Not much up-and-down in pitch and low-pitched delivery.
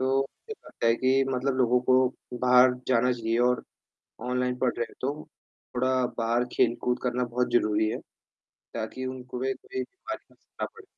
Yes: narrow, 1.2 semitones; low, 125 Hz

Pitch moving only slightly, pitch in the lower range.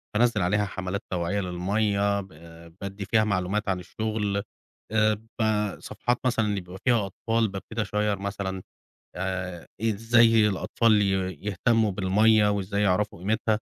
Yes: narrow, 2.3 semitones; low, 105 Hz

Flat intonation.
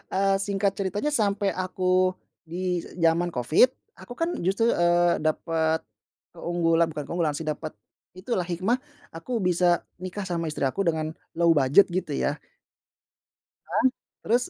No: average, 3.0 semitones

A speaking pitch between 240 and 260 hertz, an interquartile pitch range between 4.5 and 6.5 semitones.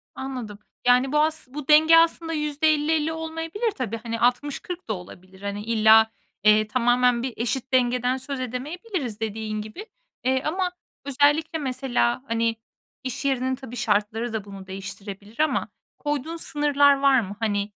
Yes: very high, 255 Hz; average, 5.3 semitones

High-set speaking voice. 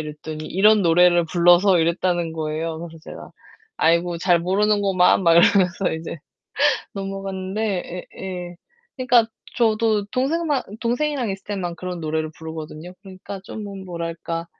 No: medium, 180 Hz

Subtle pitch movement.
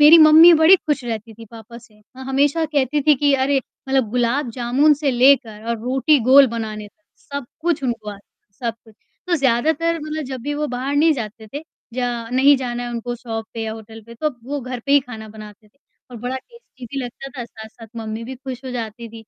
No: average, 3.8 semitones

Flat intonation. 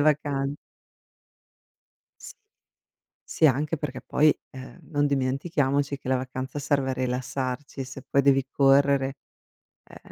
Yes: narrow, 1.6 semitones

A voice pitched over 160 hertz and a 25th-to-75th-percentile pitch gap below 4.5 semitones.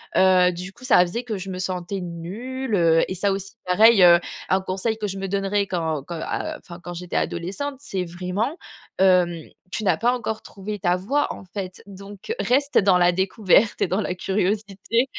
Yes: high, 190 Hz; average, 2.8 semitones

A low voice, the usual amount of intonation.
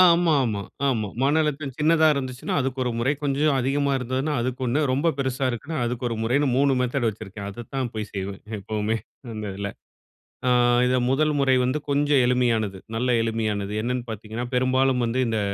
Yes: low, 125 Hz; average, 3.5 semitones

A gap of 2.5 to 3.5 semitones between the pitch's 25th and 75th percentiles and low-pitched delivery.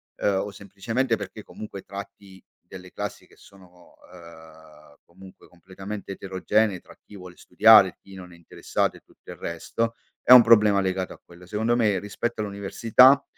Yes: average, 2.8 semitones; low, 100 Hz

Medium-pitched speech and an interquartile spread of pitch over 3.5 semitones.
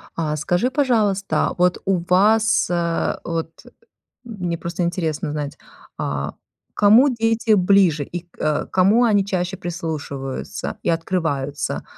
Yes: medium, 175 Hz; average, 4.0 semitones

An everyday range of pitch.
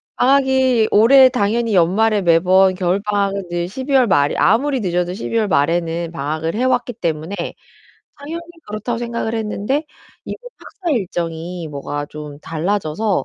No: wide, 5.8 semitones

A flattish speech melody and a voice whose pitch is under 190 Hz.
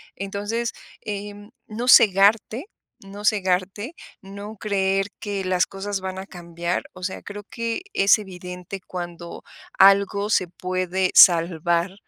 No: narrow, 2.0 semitones; high, 195 Hz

